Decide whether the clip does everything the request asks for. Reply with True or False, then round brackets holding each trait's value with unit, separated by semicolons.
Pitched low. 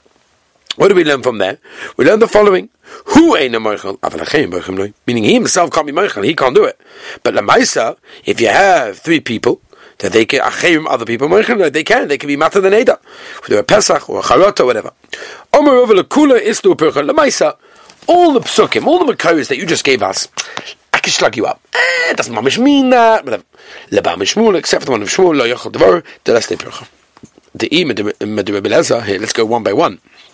False (335 Hz)